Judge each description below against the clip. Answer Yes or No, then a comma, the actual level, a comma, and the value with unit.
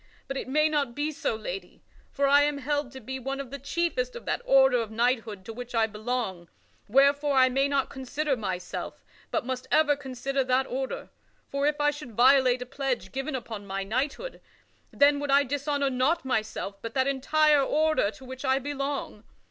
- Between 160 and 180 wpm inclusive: No, average, 195 wpm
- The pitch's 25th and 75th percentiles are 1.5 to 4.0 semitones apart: Yes, average, 2.7 semitones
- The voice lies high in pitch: Yes, very high, 265 Hz